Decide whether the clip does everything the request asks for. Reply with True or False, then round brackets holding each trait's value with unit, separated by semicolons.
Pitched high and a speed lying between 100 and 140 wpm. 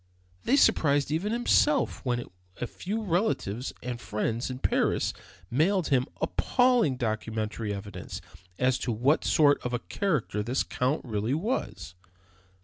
False (130 Hz; 135 wpm)